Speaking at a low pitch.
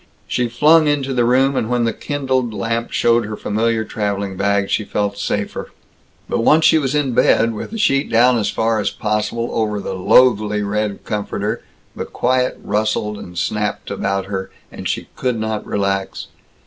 Yes: low, 110 Hz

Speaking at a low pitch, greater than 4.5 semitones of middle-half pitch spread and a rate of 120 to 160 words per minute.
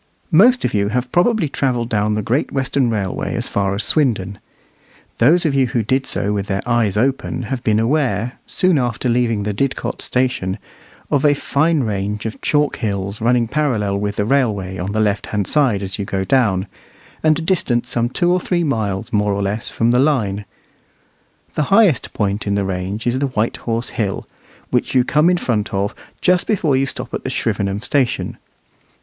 No: low, 115 Hz; average, 5.2 semitones; average, 190 wpm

